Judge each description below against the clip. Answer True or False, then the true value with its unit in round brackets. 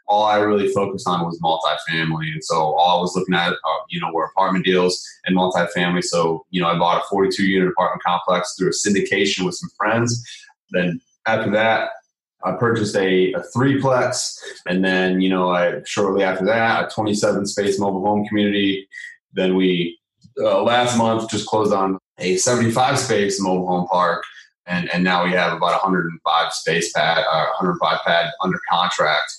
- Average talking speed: True (175 wpm)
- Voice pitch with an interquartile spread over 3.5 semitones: False (3.0 semitones)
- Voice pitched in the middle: False (95 Hz)